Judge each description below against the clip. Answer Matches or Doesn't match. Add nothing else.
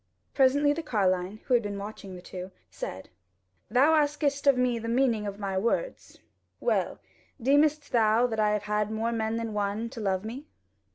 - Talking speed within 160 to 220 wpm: Matches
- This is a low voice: Doesn't match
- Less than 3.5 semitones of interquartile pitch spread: Doesn't match